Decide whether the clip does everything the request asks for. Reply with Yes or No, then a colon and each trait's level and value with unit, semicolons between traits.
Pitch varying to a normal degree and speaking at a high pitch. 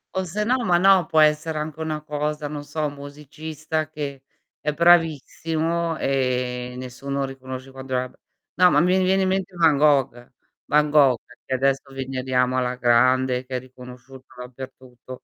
No: average, 3.5 semitones; medium, 145 Hz